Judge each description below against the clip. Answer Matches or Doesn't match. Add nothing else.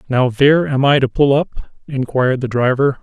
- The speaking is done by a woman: Doesn't match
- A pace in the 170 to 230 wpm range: Matches